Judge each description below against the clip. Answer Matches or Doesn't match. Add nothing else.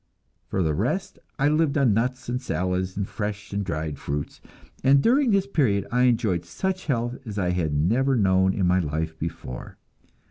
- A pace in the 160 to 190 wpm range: Matches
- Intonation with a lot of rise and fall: Matches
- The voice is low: Matches